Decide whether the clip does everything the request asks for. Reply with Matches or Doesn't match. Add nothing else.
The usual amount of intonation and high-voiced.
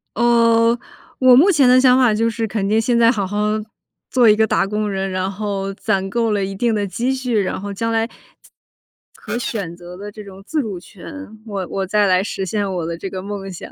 Matches